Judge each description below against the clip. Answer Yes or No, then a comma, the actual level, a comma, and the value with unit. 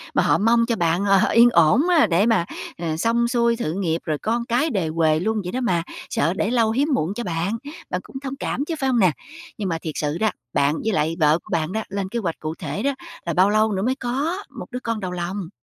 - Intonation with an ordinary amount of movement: No, wide, 5.8 semitones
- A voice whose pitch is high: Yes, high, 205 Hz